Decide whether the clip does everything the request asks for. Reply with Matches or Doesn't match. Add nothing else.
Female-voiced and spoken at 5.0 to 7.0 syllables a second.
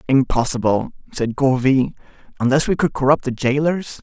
Doesn't match